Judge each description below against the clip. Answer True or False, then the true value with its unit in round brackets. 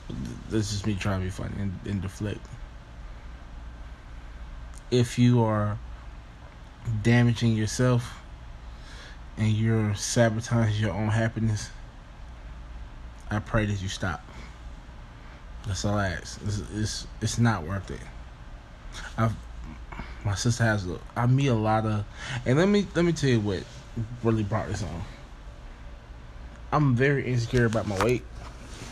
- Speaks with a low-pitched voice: True (105 Hz)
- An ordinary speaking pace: False (130 wpm)